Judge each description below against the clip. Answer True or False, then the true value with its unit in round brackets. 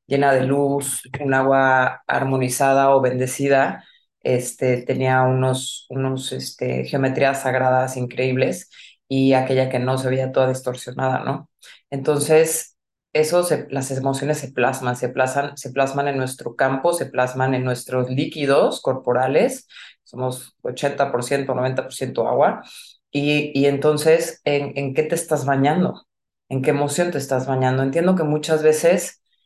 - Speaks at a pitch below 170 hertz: True (135 Hz)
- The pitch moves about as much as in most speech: False (1.7 semitones)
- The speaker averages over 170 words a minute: False (140 wpm)